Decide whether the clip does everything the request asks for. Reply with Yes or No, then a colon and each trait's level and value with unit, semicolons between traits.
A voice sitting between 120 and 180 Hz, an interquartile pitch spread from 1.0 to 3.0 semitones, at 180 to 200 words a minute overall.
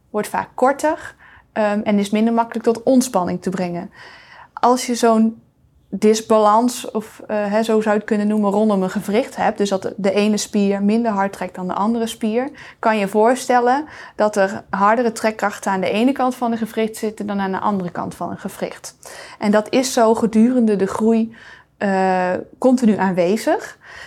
No: high, 220 Hz; narrow, 2.6 semitones; average, 185 wpm